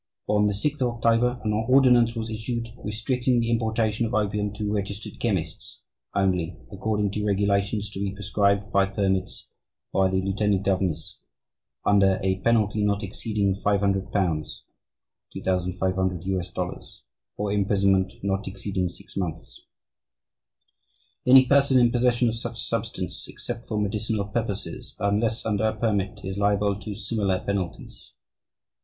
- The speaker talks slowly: Yes, slow, 125 wpm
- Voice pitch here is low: Yes, low, 105 Hz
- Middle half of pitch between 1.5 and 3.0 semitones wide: Yes, narrow, 2.5 semitones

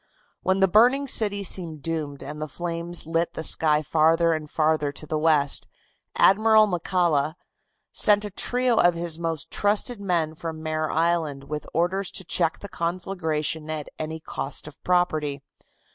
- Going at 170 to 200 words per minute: No, average, 160 wpm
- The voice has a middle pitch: Yes, medium, 165 Hz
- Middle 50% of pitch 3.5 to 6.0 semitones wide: No, average, 3.1 semitones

